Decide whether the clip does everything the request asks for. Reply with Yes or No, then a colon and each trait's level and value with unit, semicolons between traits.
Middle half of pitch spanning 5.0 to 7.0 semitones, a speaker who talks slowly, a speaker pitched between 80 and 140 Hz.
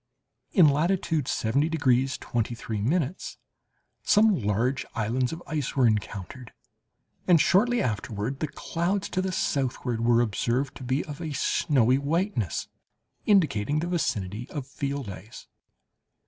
Yes: wide, 5.6 semitones; slow, 125 wpm; low, 135 Hz